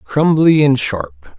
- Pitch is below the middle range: Yes, low, 130 Hz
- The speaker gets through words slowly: Yes, slow, 130 wpm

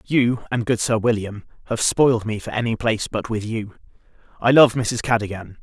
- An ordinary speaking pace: Yes, average, 190 wpm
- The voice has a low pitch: Yes, low, 115 Hz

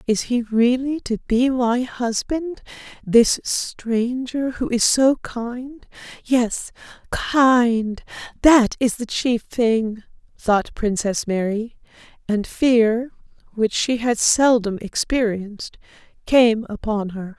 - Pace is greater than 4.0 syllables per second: No, 3.1 syllables/s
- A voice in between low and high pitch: No, high, 235 Hz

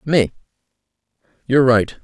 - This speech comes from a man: Yes, male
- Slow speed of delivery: Yes, slow, 90 wpm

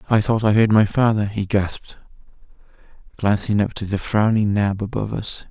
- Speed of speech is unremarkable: Yes, average, 175 wpm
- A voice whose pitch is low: Yes, low, 105 Hz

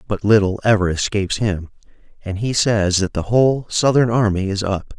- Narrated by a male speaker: Yes, male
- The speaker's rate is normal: Yes, average, 180 wpm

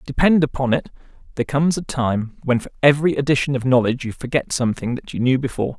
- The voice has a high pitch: No, low, 130 Hz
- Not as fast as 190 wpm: No, fast, 205 wpm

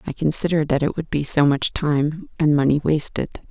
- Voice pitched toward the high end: No, medium, 155 Hz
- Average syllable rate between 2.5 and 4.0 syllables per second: No, 5.4 syllables/s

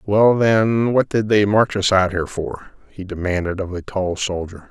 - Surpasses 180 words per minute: Yes, fast, 205 wpm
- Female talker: No, male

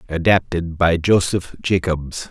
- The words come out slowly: Yes, slow, 105 wpm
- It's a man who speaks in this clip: Yes, male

